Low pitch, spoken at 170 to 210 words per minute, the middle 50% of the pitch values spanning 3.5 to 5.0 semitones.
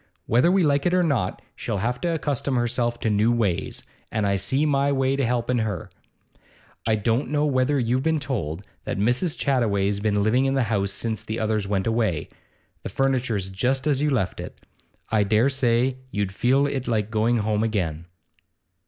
Yes: low, 120 Hz; average, 190 wpm; average, 4.4 semitones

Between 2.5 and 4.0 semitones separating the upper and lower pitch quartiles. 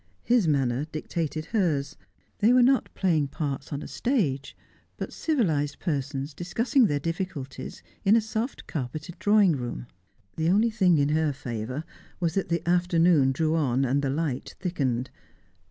No: average, 5.2 semitones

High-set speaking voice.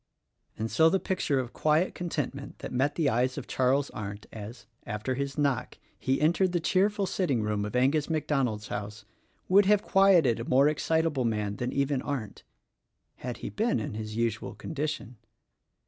No: low, 135 Hz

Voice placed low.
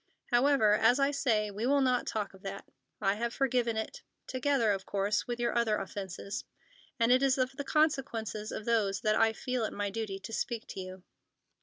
No: high, 225 Hz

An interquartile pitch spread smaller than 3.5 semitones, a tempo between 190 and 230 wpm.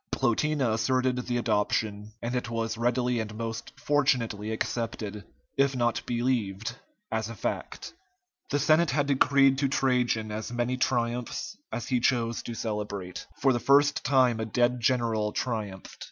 No: average, 2.7 semitones; average, 150 wpm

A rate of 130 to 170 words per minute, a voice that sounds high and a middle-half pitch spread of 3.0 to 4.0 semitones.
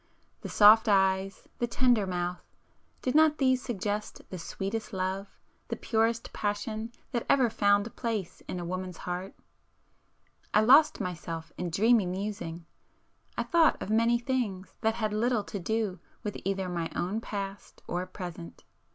Yes: average, 140 wpm; high, 205 Hz; average, 3.7 semitones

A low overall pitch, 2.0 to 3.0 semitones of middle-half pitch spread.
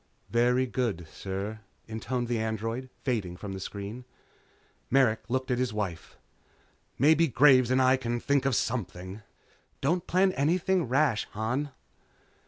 No: low, 120 Hz; average, 3.6 semitones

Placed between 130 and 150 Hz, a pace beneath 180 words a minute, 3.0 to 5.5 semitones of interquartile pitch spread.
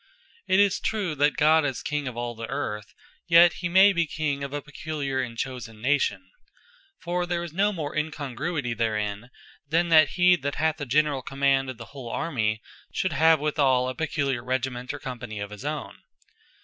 No: medium, 140 Hz; average, 190 wpm; average, 4.2 semitones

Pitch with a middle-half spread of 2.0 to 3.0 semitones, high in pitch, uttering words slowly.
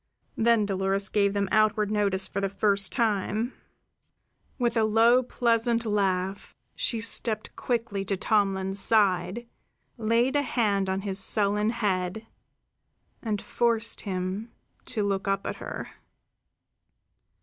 Yes: average, 2.7 semitones; high, 210 Hz; slow, 125 wpm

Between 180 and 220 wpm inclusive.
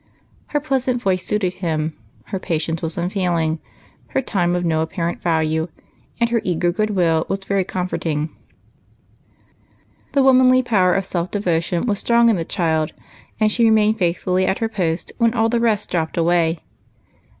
No: average, 165 wpm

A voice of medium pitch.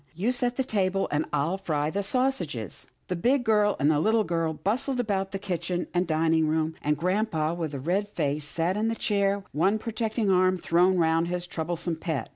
Yes: medium, 180 Hz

